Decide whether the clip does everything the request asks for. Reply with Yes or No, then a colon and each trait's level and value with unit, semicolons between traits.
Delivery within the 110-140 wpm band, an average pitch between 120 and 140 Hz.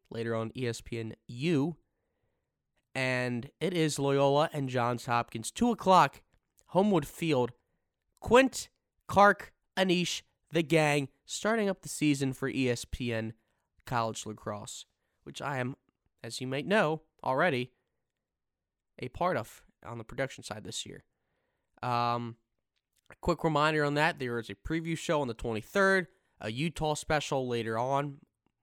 Yes: slow, 135 wpm; low, 135 Hz